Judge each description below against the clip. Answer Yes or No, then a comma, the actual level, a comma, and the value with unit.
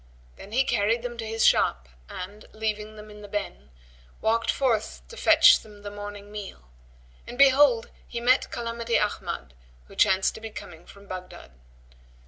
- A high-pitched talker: Yes, high, 210 Hz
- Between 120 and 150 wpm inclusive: No, average, 165 wpm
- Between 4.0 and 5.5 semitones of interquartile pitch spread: No, average, 2.8 semitones